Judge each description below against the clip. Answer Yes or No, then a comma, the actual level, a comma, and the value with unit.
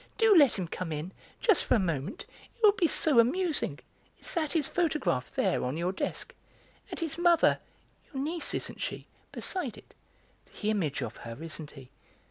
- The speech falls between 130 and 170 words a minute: No, average, 180 wpm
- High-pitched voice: Yes, high, 245 Hz